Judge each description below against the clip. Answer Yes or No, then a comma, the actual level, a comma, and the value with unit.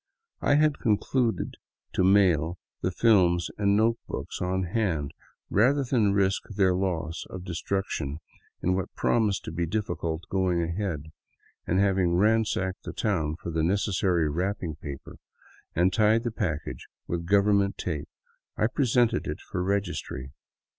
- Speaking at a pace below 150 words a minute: Yes, average, 140 wpm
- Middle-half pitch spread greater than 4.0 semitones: No, average, 3.6 semitones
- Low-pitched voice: Yes, very low, 95 Hz